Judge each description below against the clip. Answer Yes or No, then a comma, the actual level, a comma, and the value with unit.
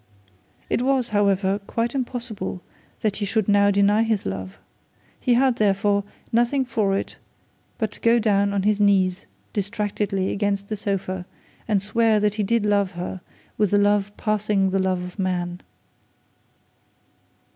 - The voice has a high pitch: Yes, high, 205 Hz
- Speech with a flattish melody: Yes, narrow, 2.0 semitones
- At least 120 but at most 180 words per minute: Yes, average, 150 wpm